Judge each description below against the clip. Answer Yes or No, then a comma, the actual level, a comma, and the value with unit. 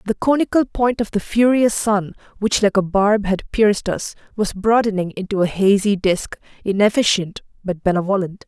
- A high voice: Yes, high, 205 Hz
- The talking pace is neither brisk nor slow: Yes, average, 165 wpm